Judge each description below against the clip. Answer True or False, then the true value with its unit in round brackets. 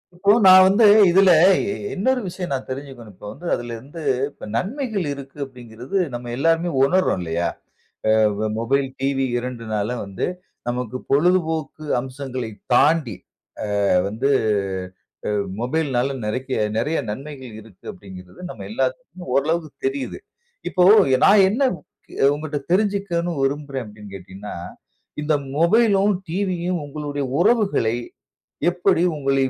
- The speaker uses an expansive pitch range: True (6.6 semitones)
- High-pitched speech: False (140 Hz)